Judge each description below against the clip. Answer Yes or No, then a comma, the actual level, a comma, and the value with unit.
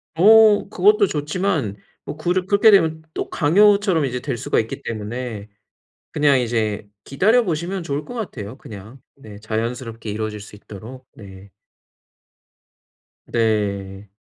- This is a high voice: No, low, 130 Hz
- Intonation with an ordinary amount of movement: No, wide, 8.8 semitones